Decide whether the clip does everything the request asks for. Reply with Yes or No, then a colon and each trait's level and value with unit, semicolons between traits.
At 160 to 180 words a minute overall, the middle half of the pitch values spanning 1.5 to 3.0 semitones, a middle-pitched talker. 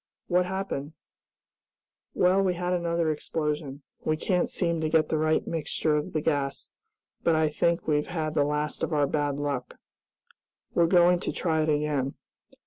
Yes: average, 165 wpm; narrow, 2.5 semitones; medium, 155 Hz